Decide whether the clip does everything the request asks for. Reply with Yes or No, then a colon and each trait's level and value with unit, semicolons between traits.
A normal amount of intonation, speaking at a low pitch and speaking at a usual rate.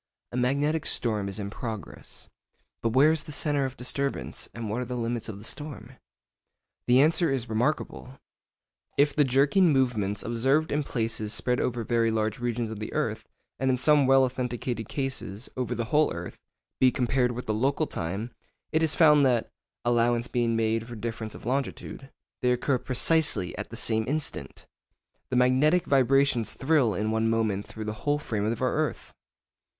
Yes: average, 3.7 semitones; low, 125 Hz; average, 175 wpm